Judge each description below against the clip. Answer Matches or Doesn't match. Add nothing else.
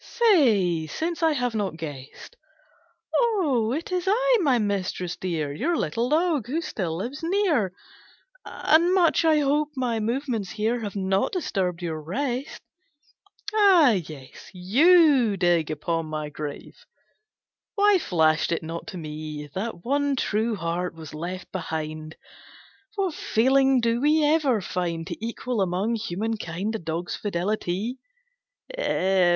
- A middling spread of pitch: Doesn't match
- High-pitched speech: Matches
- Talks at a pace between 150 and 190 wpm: Doesn't match